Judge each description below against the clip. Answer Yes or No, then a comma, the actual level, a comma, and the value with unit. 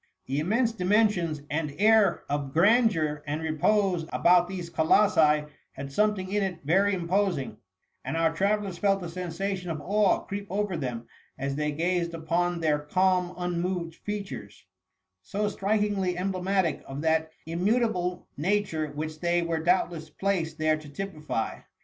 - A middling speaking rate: Yes, average, 145 wpm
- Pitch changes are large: No, average, 4.0 semitones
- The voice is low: No, medium, 175 Hz